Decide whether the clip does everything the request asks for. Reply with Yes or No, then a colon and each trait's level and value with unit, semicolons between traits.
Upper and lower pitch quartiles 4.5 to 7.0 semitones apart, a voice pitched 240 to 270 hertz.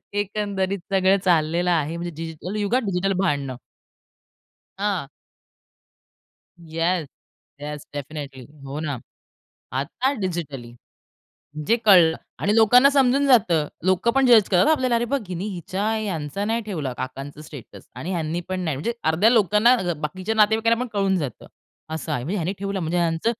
No: average, 5.0 semitones; medium, 185 Hz